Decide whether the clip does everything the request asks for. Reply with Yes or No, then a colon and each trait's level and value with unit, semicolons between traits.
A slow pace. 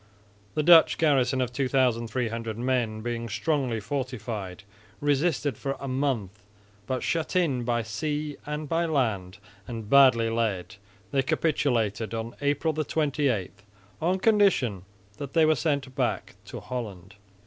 Yes: slow, 130 wpm